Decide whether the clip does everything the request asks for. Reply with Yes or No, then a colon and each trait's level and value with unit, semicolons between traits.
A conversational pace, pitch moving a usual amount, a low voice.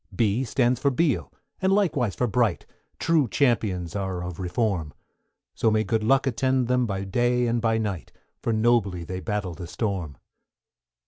Yes: average, 160 wpm; average, 4.6 semitones; low, 110 Hz